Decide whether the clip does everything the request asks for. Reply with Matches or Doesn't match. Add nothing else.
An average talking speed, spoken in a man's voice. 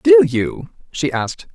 Matches